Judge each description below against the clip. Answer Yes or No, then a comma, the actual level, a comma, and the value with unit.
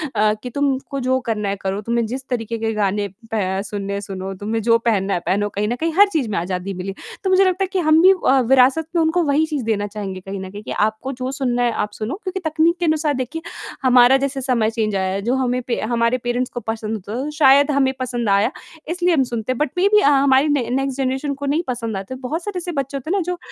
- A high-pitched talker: Yes, very high, 250 Hz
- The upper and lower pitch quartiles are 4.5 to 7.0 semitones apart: Yes, average, 5.2 semitones